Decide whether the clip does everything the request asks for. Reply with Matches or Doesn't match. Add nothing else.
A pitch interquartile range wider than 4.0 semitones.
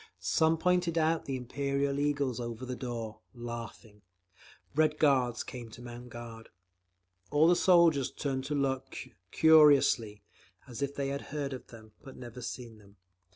Doesn't match